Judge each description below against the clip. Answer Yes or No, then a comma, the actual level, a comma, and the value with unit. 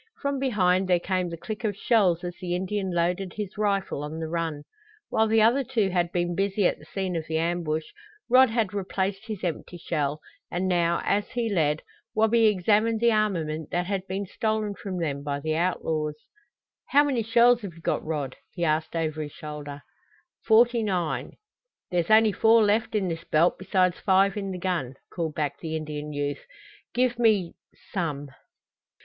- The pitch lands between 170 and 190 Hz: Yes, medium, 185 Hz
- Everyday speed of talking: Yes, average, 180 wpm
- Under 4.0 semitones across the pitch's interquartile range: No, average, 4.7 semitones